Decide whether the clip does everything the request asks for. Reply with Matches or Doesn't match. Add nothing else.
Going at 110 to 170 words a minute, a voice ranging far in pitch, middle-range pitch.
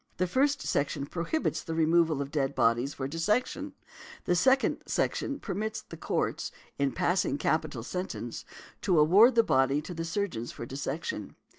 Matches